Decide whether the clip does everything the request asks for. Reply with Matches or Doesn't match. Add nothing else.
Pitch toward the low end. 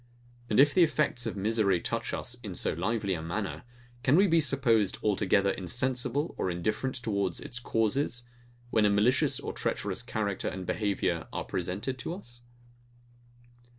Matches